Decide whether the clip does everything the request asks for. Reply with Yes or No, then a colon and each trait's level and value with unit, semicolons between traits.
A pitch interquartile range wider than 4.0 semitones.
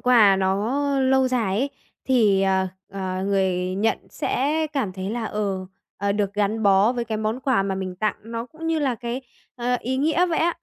Yes: average, 5.0 semitones